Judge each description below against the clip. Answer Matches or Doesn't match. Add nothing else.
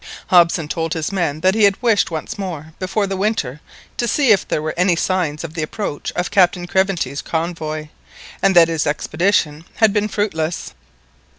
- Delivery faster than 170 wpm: Matches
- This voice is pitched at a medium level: Matches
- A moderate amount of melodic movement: Matches